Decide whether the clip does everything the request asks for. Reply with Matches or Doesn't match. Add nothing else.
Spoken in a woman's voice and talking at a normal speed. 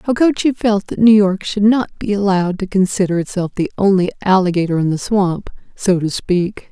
Matches